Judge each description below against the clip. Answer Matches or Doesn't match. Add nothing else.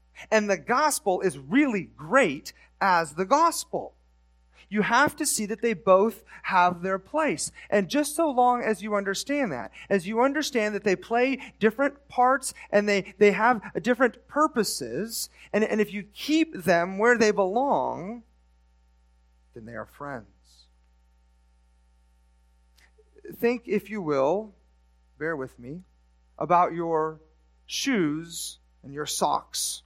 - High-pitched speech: Matches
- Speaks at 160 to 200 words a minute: Doesn't match